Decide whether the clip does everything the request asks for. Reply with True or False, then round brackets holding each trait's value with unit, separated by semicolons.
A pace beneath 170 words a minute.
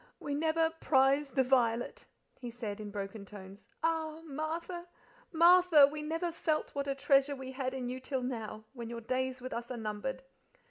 False (180 wpm)